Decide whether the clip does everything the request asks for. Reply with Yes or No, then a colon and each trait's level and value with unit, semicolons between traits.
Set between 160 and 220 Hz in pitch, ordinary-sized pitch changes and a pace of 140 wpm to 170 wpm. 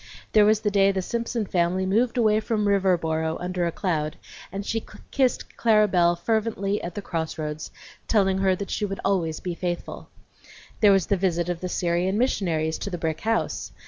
No: high, 190 Hz; average, 3.5 semitones; average, 190 wpm